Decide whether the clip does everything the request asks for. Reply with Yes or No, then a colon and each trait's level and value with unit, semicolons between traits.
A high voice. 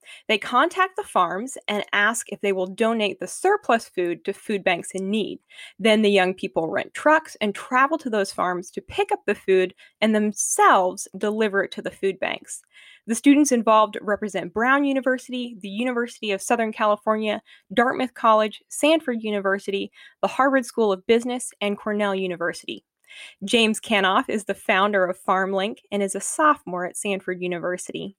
Yes: high, 215 Hz